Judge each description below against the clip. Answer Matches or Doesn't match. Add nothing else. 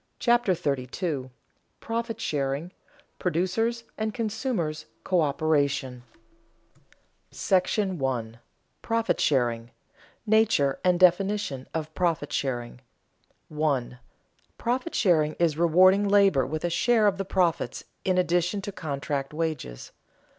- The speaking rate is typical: Doesn't match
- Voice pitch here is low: Doesn't match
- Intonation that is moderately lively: Doesn't match